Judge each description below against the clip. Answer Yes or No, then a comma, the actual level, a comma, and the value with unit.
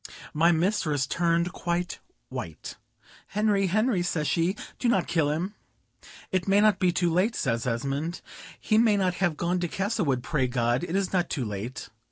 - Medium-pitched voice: Yes, medium, 175 Hz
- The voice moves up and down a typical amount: Yes, average, 4.6 semitones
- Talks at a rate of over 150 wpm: Yes, average, 175 wpm